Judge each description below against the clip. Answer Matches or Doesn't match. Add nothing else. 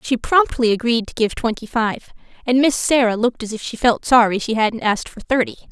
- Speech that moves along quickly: Matches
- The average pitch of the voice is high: Matches